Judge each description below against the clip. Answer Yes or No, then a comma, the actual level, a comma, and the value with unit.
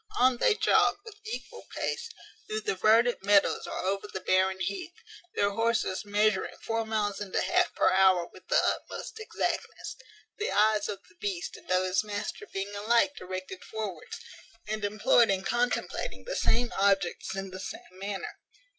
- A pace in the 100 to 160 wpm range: No, average, 170 wpm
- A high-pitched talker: Yes, high, 205 Hz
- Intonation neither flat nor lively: Yes, average, 3.1 semitones